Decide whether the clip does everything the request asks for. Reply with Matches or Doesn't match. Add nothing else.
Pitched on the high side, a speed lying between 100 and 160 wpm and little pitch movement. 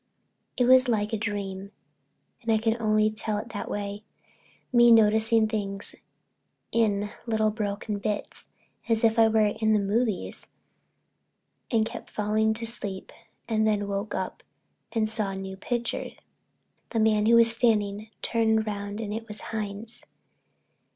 Matches